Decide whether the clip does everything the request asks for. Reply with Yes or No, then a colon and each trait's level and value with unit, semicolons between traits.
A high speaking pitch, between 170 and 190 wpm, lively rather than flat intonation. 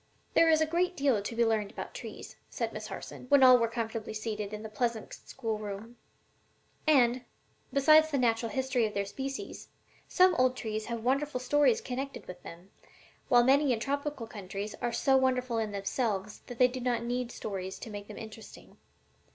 No: high, 240 Hz; average, 185 wpm; average, 3.7 semitones